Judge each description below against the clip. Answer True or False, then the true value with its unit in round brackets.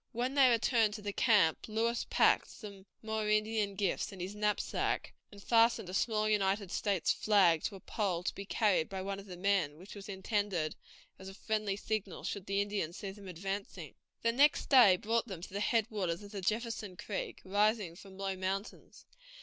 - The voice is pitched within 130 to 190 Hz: False (200 Hz)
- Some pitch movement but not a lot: False (2.1 semitones)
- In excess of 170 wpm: True (195 wpm)